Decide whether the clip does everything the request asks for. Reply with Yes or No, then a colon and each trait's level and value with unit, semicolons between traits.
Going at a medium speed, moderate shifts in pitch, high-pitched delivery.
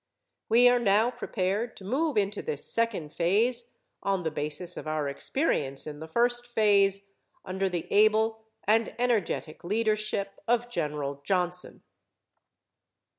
No: slow, 130 wpm; average, 5.0 semitones; high, 200 Hz